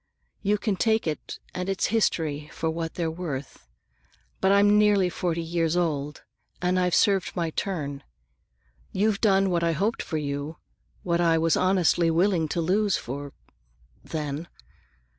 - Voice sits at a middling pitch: Yes, medium, 170 Hz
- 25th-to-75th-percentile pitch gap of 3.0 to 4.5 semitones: Yes, average, 3.6 semitones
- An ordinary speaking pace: Yes, average, 150 wpm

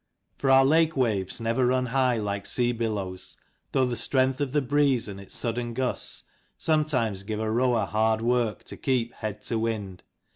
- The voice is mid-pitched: No, low, 120 Hz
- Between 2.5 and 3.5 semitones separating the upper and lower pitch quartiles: Yes, average, 3.2 semitones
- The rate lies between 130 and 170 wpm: No, average, 190 wpm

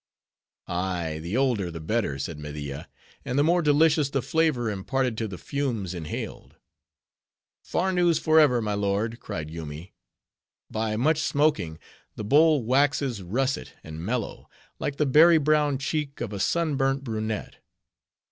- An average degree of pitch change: No, wide, 7.5 semitones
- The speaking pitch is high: No, low, 120 Hz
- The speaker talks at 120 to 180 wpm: Yes, average, 140 wpm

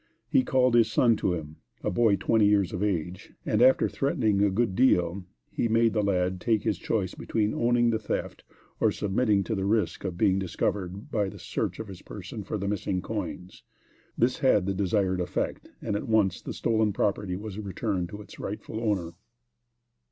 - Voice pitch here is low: Yes, low, 105 Hz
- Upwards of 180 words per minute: Yes, average, 190 wpm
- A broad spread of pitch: No, average, 3.0 semitones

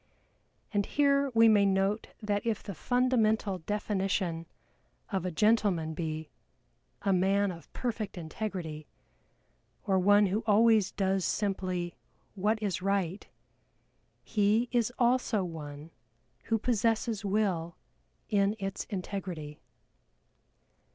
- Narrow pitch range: No, average, 3.2 semitones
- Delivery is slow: Yes, slow, 110 wpm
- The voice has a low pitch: No, high, 200 Hz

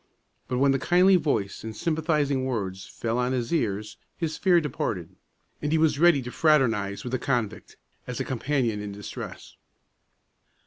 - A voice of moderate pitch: No, low, 130 Hz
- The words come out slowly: No, average, 165 wpm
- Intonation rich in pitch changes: Yes, wide, 6.0 semitones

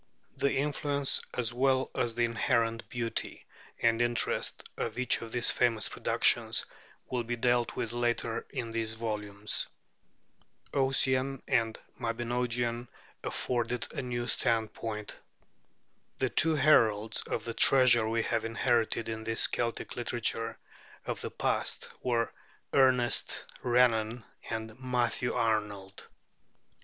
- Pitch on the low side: Yes, low, 120 Hz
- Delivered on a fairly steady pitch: Yes, narrow, 1.6 semitones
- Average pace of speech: No, slow, 120 wpm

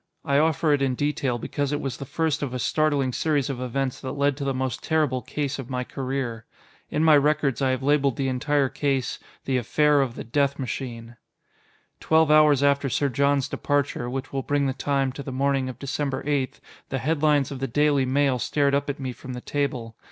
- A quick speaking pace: Yes, fast, 210 wpm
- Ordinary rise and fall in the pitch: No, narrow, 1.9 semitones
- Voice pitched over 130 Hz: Yes, medium, 140 Hz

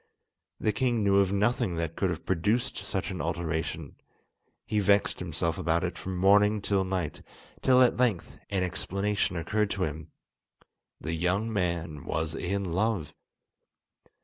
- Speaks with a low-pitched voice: Yes, very low, 95 Hz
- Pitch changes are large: No, average, 3.6 semitones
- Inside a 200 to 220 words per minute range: No, average, 145 wpm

